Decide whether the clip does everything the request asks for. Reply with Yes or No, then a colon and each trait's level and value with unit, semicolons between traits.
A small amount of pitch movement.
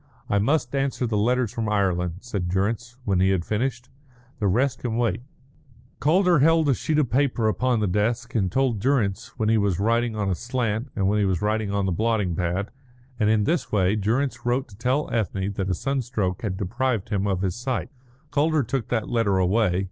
No: average, 4.2 semitones